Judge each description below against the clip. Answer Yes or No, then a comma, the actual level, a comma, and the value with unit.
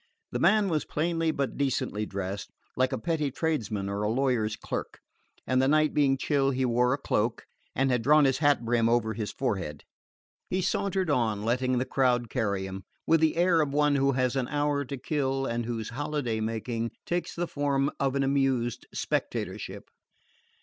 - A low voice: Yes, low, 130 Hz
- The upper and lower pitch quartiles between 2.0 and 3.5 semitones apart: No, average, 4.0 semitones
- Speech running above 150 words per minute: Yes, average, 185 wpm